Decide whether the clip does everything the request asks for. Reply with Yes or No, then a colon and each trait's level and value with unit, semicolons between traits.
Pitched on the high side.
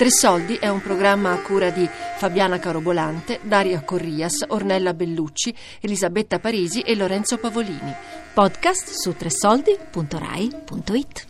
Yes: high, 195 Hz